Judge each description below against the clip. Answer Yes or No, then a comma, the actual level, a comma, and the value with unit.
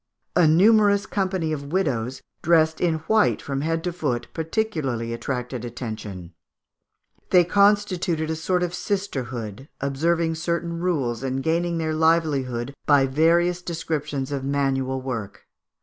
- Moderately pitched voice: Yes, medium, 155 Hz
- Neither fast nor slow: No, slow, 130 wpm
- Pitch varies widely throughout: No, average, 4.6 semitones